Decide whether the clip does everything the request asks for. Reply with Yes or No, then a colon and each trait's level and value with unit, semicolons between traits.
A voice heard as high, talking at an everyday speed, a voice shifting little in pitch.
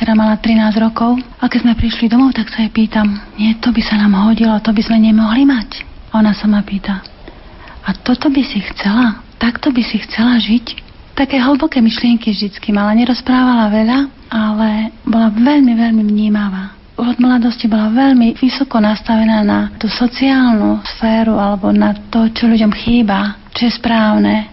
No: high, 225 Hz; fast, 170 wpm; narrow, 2.1 semitones